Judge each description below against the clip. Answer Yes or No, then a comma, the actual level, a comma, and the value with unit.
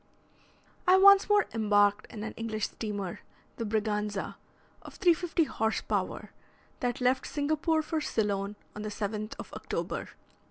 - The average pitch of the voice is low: No, high, 220 Hz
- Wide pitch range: Yes, wide, 6.8 semitones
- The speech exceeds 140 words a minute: No, slow, 135 wpm